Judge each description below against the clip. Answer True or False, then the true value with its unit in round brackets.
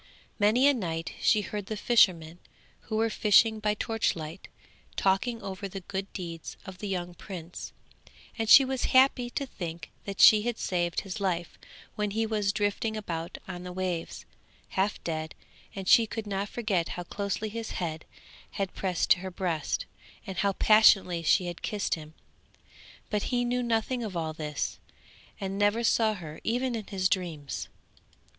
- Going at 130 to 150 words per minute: False (165 wpm)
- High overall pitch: True (195 Hz)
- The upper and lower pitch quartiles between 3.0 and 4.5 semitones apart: True (3.8 semitones)